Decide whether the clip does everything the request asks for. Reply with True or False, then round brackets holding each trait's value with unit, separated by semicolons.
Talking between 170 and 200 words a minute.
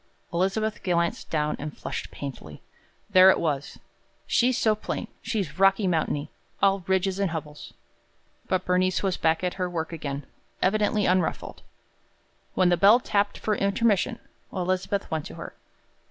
False (145 wpm)